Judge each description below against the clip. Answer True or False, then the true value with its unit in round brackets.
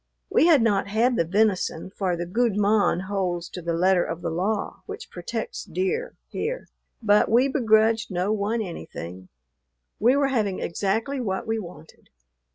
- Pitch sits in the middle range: False (210 Hz)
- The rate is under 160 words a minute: False (165 wpm)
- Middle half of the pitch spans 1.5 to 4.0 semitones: False (4.7 semitones)